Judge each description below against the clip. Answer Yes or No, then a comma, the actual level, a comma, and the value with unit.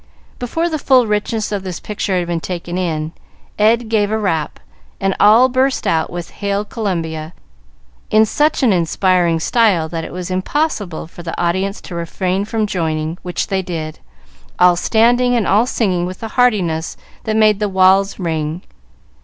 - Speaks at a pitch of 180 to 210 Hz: Yes, high, 190 Hz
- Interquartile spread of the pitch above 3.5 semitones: Yes, average, 4.2 semitones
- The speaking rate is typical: Yes, average, 170 wpm